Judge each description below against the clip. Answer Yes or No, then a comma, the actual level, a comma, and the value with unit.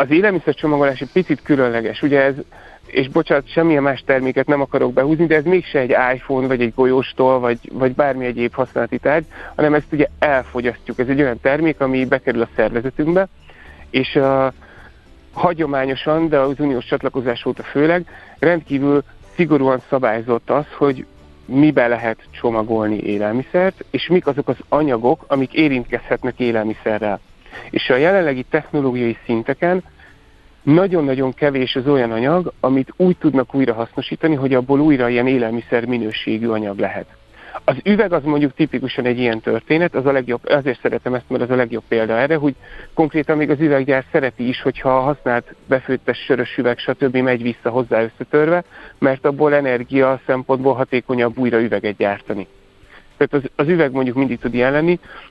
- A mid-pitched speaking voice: No, low, 130 Hz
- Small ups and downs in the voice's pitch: No, average, 3.5 semitones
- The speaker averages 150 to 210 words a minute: Yes, fast, 155 wpm